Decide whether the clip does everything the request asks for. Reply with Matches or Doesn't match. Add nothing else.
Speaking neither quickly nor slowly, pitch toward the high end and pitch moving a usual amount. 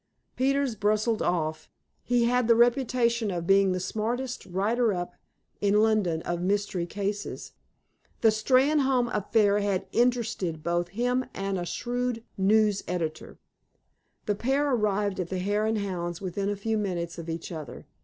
Matches